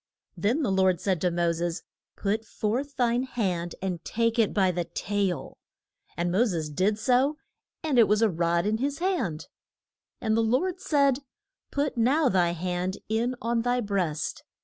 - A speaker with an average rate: Yes, average, 170 wpm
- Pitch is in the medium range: No, high, 210 Hz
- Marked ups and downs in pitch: Yes, wide, 5.8 semitones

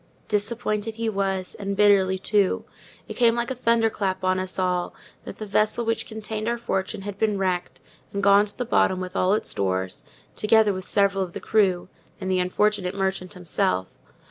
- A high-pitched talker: Yes, high, 200 Hz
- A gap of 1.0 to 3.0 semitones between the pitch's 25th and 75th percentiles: Yes, narrow, 2.5 semitones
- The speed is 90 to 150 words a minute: No, average, 190 wpm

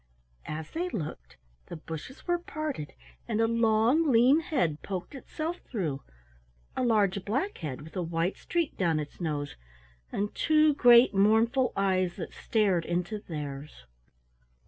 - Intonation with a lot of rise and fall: Yes, wide, 8.0 semitones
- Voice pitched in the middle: No, high, 205 Hz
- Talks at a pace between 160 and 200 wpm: No, average, 145 wpm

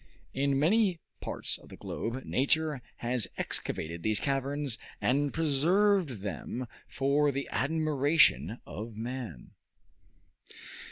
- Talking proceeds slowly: Yes, slow, 105 wpm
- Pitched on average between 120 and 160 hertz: Yes, low, 135 Hz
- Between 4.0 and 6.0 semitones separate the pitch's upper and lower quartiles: Yes, average, 4.3 semitones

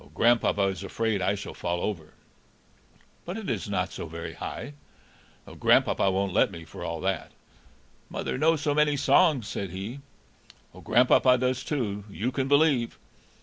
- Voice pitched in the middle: No, low, 110 Hz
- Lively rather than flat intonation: Yes, wide, 6.1 semitones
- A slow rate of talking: No, average, 150 wpm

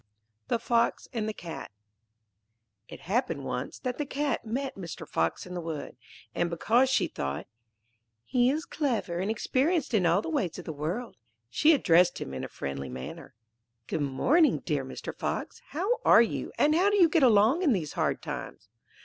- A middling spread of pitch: No, wide, 8.9 semitones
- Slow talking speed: No, average, 185 wpm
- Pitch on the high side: Yes, high, 220 Hz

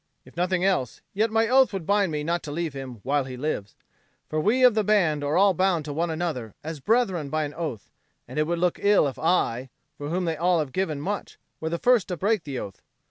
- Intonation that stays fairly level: No, average, 4.8 semitones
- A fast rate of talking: Yes, fast, 245 wpm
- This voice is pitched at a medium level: Yes, medium, 165 Hz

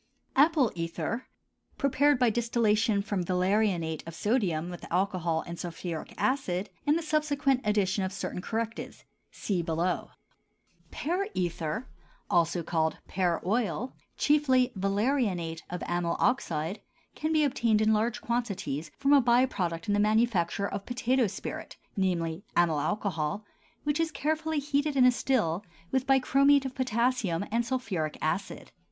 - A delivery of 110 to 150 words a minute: Yes, average, 140 wpm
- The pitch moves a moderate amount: No, wide, 6.8 semitones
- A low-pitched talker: No, high, 210 Hz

